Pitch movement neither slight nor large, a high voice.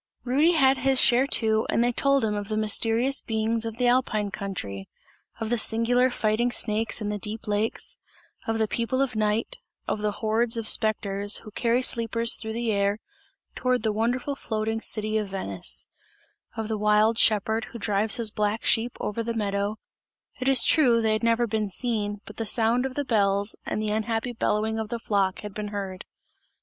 No: narrow, 2.0 semitones; high, 220 Hz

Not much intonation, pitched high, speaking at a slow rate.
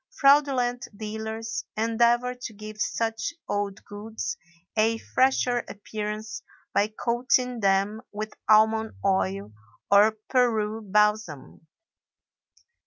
Yes: narrow, 2.2 semitones; high, 220 Hz; slow, 95 wpm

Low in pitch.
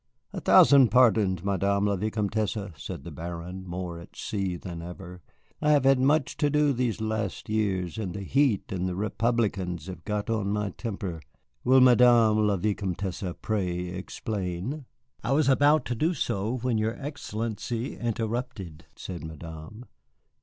Yes: low, 105 Hz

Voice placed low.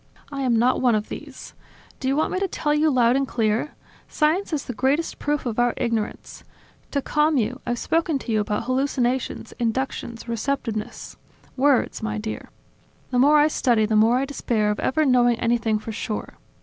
No: very high, 250 Hz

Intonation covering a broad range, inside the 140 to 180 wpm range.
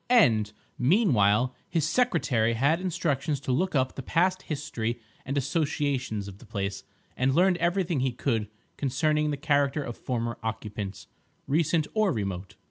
Yes: wide, 5.8 semitones; average, 145 wpm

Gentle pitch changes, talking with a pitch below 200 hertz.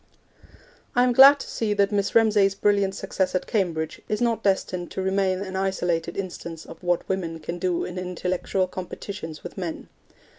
Yes: narrow, 2.3 semitones; high, 190 Hz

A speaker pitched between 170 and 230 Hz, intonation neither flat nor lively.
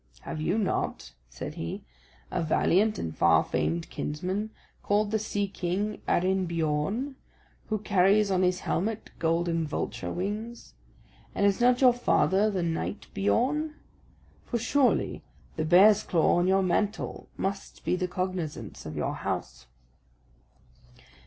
Yes: high, 190 Hz; average, 3.9 semitones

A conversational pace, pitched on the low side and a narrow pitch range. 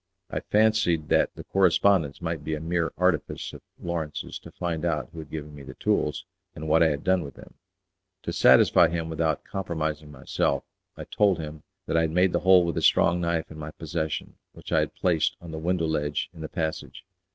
No: fast, 210 wpm; very low, 80 Hz; narrow, 2.1 semitones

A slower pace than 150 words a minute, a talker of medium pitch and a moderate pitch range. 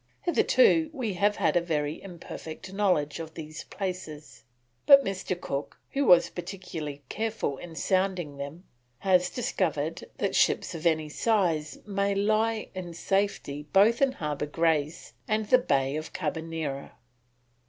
Yes: average, 140 wpm; medium, 175 Hz; average, 4.7 semitones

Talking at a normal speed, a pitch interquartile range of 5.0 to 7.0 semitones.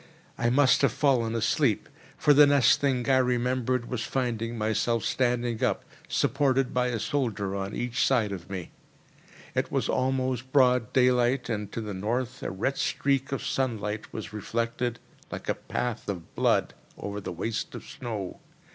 No: average, 165 wpm; average, 3.0 semitones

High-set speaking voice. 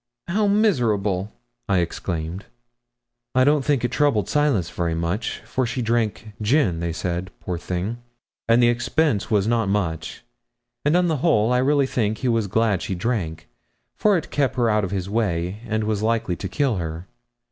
No: low, 110 Hz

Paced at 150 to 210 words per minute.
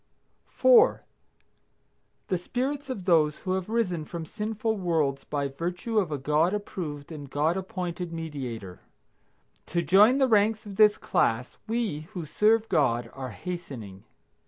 No: average, 140 wpm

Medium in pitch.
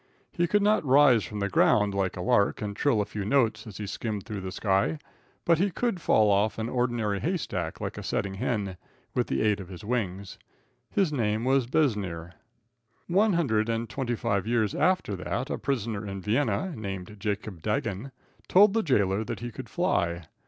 No: low, 110 Hz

